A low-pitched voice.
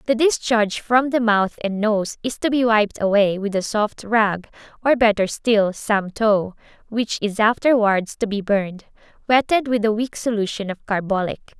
No: high, 215 Hz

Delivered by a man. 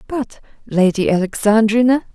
No: female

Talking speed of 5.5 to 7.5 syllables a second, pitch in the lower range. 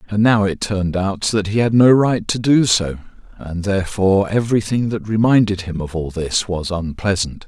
No: 5.1 syllables/s; low, 100 Hz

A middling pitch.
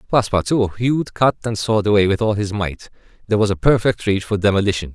No: low, 105 Hz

